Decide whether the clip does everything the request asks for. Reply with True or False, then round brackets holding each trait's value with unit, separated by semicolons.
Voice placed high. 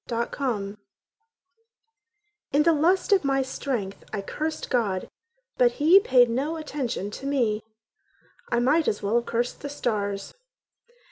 True (255 Hz)